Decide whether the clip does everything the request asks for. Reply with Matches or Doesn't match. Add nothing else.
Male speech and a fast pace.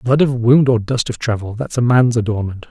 Matches